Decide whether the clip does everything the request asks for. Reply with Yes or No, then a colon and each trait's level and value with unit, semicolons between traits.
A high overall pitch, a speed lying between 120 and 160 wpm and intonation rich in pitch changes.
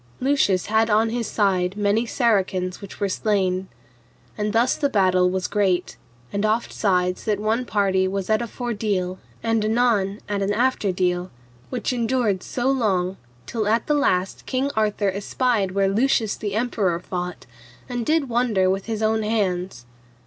No: high, 210 Hz; average, 155 wpm; average, 3.4 semitones